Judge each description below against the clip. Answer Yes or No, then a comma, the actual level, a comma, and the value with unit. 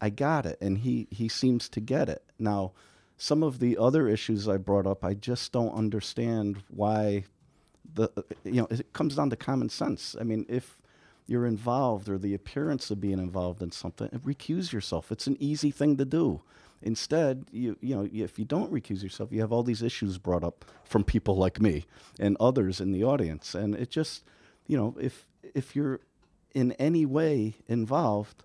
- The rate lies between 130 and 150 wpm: No, average, 190 wpm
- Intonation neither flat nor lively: Yes, average, 4.5 semitones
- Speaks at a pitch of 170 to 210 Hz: No, low, 110 Hz